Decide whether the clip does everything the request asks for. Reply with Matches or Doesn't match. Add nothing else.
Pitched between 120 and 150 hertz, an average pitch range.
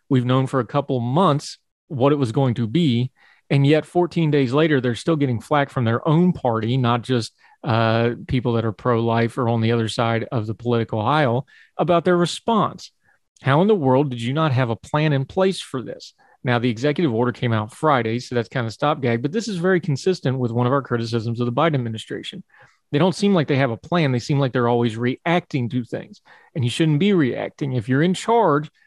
Matches